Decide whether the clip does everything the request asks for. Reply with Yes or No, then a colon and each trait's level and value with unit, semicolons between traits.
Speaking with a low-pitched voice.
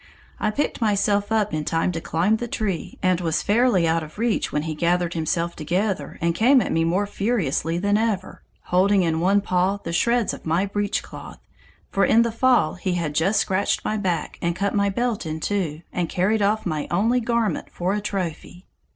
No: high, 190 Hz